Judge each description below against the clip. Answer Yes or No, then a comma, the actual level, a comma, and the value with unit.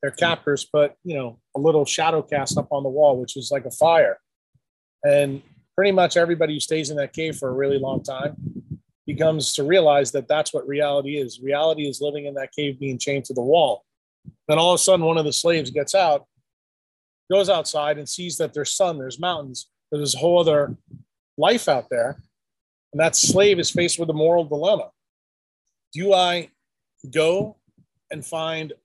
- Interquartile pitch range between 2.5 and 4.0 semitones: Yes, average, 2.9 semitones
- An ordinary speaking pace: Yes, average, 190 wpm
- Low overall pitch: No, medium, 150 Hz